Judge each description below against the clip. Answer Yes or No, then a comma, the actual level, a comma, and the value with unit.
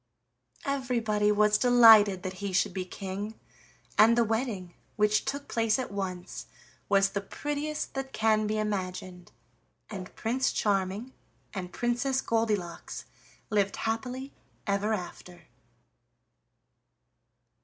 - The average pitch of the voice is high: Yes, high, 210 Hz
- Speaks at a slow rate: Yes, slow, 110 wpm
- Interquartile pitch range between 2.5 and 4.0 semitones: Yes, average, 3.5 semitones